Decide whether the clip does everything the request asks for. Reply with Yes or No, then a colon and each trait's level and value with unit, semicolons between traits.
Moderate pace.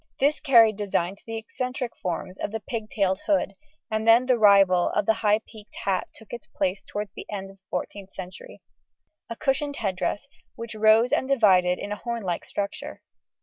Yes: average, 190 wpm